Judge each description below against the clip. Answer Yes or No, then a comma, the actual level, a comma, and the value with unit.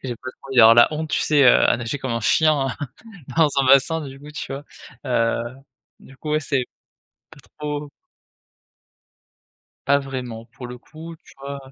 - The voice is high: No, low, 135 Hz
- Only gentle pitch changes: No, average, 3.2 semitones